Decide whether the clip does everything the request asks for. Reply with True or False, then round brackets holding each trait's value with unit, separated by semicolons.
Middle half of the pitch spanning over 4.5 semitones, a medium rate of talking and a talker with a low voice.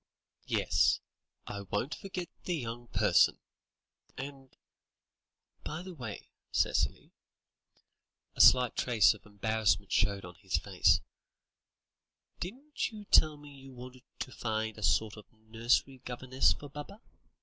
False (4.9 semitones; 125 wpm; 125 Hz)